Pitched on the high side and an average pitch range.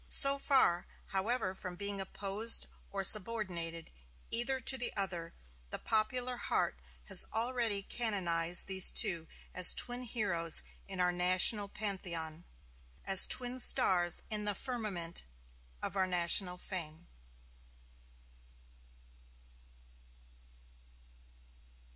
Yes: high, 195 Hz; average, 4.4 semitones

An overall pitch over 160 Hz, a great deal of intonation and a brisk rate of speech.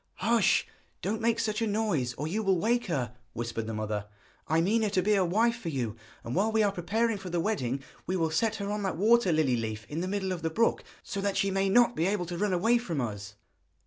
Yes: high, 190 Hz; wide, 5.7 semitones; fast, 250 wpm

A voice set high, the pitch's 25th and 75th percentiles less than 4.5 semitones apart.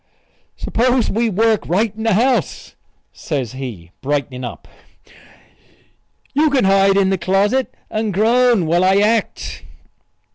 No: high, 200 Hz; average, 4.8 semitones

